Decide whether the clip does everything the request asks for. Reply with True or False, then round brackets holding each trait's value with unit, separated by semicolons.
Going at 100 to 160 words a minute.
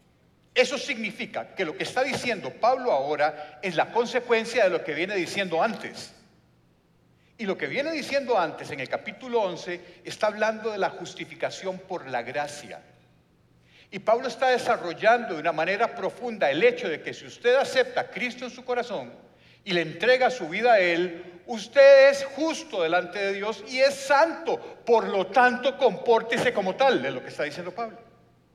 False (175 wpm)